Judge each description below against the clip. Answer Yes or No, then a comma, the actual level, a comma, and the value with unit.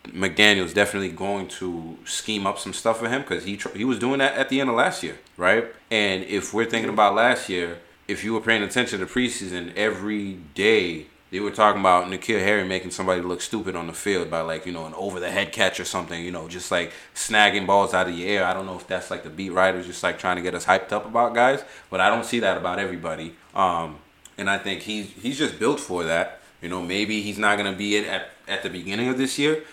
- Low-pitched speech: Yes, low, 100 Hz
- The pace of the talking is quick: Yes, fast, 255 wpm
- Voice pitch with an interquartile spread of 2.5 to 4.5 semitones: Yes, average, 2.9 semitones